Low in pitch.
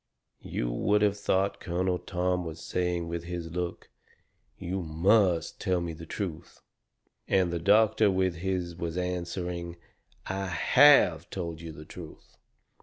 Yes: very low, 90 Hz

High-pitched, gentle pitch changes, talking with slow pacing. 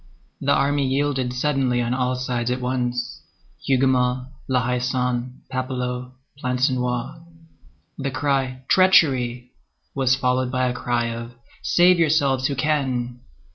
No: low, 130 Hz; narrow, 1.5 semitones; slow, 120 wpm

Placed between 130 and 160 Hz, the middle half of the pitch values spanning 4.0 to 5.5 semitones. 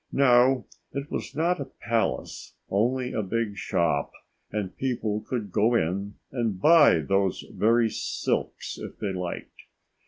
No: low, 115 Hz; average, 4.5 semitones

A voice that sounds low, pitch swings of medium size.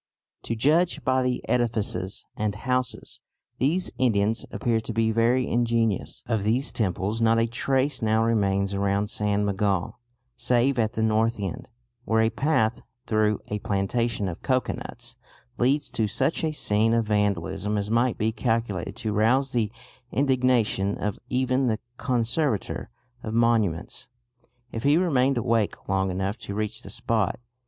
Yes: low, 115 Hz; average, 3.3 semitones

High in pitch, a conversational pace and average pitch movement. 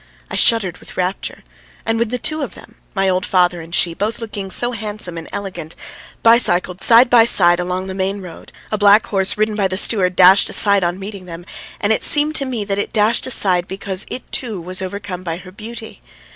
No: high, 195 Hz; fast, 215 wpm; average, 3.3 semitones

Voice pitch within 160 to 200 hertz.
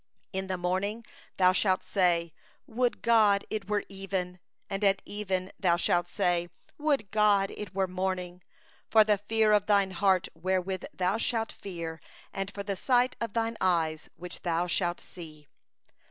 Yes: high, 190 Hz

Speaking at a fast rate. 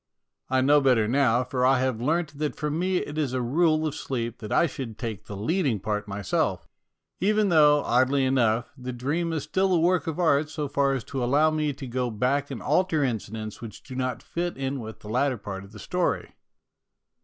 Yes: fast, 210 wpm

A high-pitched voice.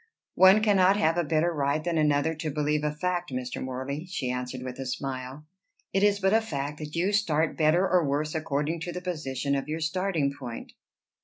No: medium, 155 Hz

